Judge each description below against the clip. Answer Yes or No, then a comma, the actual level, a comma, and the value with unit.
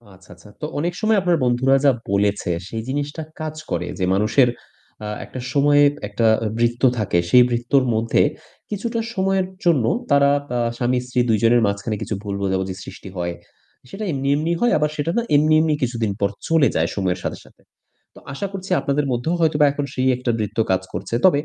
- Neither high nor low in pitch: No, low, 125 Hz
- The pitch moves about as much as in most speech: No, wide, 6.1 semitones